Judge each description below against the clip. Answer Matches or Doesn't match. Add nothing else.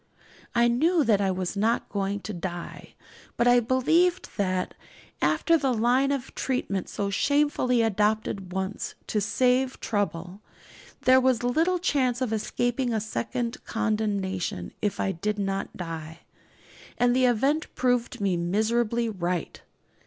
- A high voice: Matches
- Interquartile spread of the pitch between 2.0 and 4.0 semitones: Doesn't match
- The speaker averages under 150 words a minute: Matches